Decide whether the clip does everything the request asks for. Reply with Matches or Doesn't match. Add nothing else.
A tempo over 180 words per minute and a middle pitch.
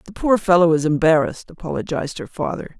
Doesn't match